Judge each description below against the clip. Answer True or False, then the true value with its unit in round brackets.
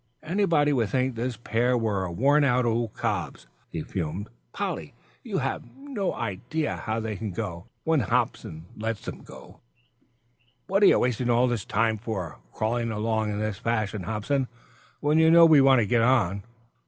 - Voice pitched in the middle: False (115 Hz)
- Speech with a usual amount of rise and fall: True (4.0 semitones)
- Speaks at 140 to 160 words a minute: False (170 wpm)